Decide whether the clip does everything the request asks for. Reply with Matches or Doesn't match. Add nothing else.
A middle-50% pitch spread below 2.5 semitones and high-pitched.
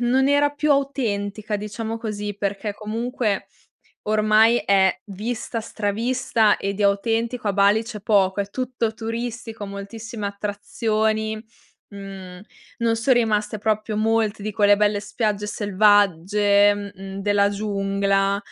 Matches